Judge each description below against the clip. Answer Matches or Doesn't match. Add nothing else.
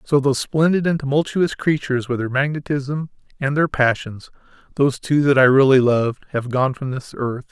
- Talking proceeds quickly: Doesn't match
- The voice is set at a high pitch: Doesn't match